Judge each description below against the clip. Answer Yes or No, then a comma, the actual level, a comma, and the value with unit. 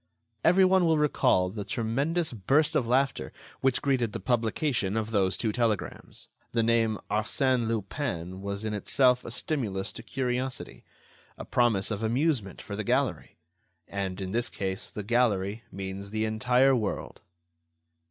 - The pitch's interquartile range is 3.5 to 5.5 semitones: Yes, average, 4.5 semitones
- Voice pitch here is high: No, low, 115 Hz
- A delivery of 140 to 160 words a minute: Yes, average, 150 wpm